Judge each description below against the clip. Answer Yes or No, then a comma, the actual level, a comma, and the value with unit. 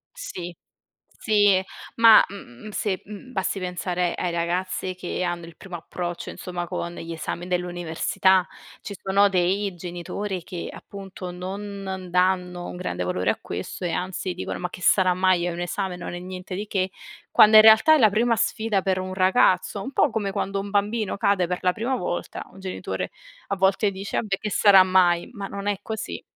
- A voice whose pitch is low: No, medium, 185 Hz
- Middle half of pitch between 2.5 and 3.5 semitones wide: No, narrow, 2.1 semitones